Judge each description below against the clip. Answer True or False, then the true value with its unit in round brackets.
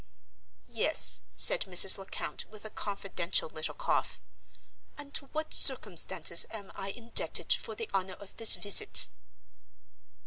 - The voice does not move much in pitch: False (3.8 semitones)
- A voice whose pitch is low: False (205 Hz)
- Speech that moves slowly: True (130 wpm)